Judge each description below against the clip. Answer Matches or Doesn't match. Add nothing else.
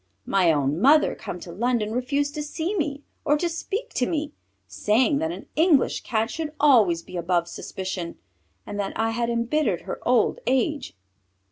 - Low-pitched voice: Doesn't match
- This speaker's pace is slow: Doesn't match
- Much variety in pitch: Matches